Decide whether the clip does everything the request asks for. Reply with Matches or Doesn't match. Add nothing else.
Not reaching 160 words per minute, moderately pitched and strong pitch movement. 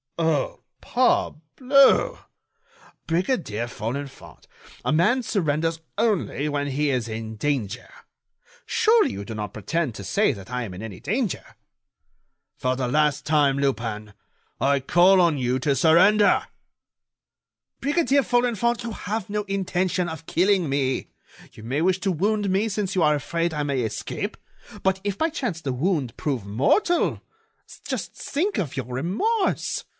Matches